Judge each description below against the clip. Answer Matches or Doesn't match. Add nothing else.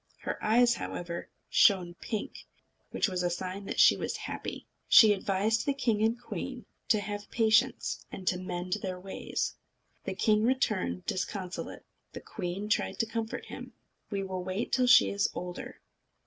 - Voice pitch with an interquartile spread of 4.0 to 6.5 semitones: Doesn't match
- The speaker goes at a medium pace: Matches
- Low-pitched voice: Doesn't match